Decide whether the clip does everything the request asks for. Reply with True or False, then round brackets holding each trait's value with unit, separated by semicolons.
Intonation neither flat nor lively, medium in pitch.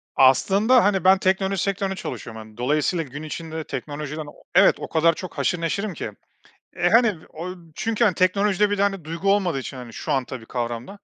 False (5.7 semitones; 170 Hz)